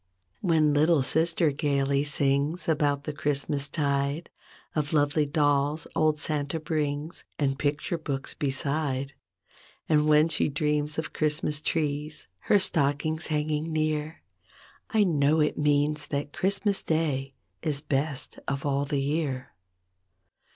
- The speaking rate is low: Yes, slow, 130 wpm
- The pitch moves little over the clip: Yes, narrow, 1.7 semitones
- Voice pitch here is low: No, medium, 150 Hz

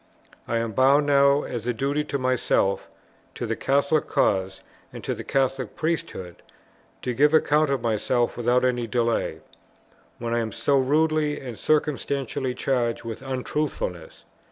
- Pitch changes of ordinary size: Yes, average, 3.4 semitones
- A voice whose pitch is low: Yes, low, 130 Hz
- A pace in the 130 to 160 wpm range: Yes, average, 145 wpm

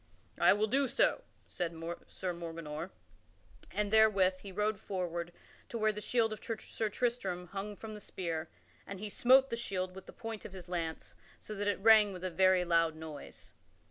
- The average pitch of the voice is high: Yes, high, 195 Hz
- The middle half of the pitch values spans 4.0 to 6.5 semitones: No, average, 3.6 semitones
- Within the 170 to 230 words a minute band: Yes, average, 185 wpm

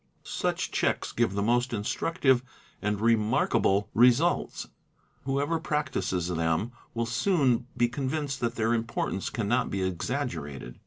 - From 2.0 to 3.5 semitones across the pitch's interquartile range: No, average, 4.6 semitones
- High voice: No, low, 120 Hz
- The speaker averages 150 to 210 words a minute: No, slow, 135 wpm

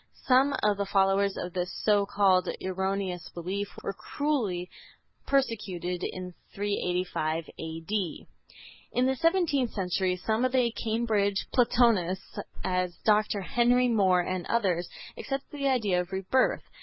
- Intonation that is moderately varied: Yes, average, 4.6 semitones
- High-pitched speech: Yes, high, 200 Hz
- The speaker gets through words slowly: Yes, slow, 130 wpm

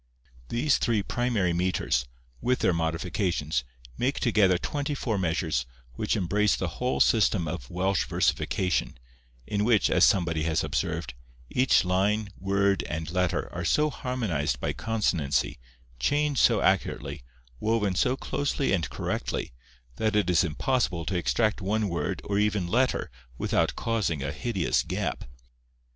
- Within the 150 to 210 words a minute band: No, average, 140 wpm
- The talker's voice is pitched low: Yes, very low, 95 Hz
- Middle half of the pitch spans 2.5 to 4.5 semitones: No, average, 5.1 semitones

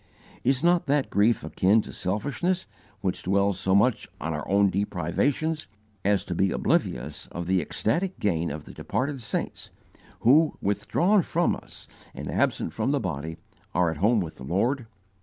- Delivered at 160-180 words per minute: Yes, average, 165 wpm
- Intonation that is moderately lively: No, wide, 7.6 semitones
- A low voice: Yes, low, 100 Hz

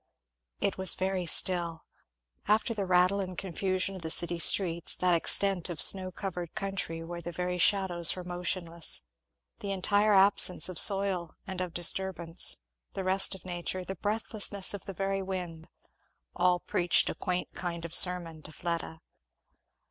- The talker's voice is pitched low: No, medium, 180 Hz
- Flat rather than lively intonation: Yes, narrow, 2.0 semitones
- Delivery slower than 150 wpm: No, average, 155 wpm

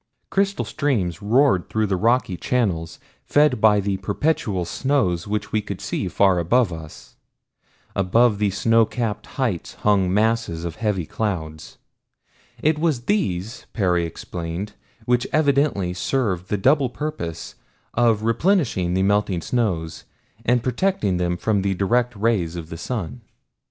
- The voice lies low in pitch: Yes, low, 105 Hz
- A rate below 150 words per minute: Yes, slow, 135 wpm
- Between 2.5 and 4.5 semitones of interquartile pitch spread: No, wide, 5.5 semitones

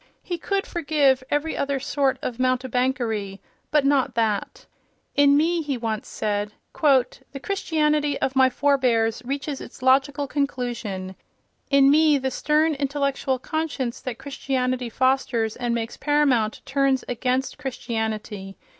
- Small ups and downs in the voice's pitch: No, average, 3.1 semitones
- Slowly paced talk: Yes, slow, 130 wpm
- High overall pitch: Yes, very high, 265 Hz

